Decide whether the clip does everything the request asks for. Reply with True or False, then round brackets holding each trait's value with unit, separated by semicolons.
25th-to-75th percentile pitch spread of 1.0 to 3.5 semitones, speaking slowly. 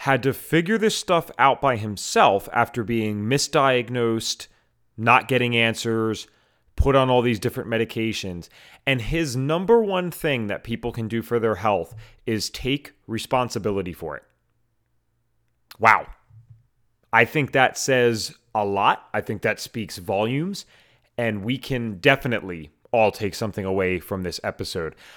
False (3.0 semitones; 145 wpm)